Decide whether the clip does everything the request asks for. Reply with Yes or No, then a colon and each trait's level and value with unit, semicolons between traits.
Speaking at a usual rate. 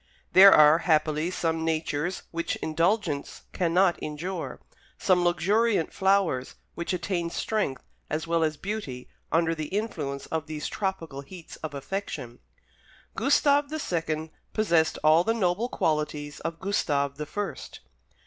No: slow, 130 wpm